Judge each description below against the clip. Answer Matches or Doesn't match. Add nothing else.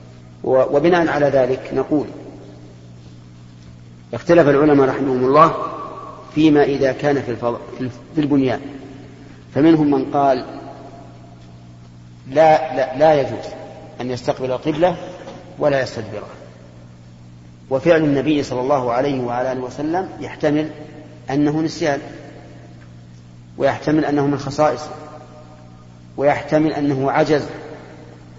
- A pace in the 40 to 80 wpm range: Doesn't match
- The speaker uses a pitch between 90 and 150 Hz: Matches